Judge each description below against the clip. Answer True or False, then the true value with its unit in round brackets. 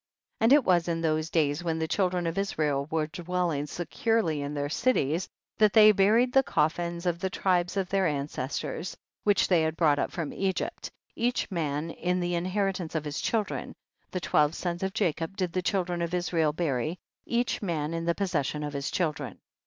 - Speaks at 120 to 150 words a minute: False (200 wpm)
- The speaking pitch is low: False (170 Hz)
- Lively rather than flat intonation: False (3.5 semitones)